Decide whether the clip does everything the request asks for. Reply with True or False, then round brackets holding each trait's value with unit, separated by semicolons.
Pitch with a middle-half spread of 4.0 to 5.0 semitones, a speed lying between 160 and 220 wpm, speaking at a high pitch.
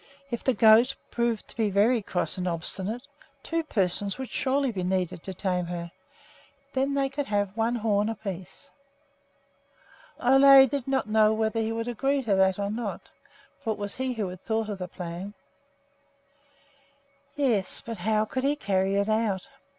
True (4.4 semitones; 170 wpm; 220 Hz)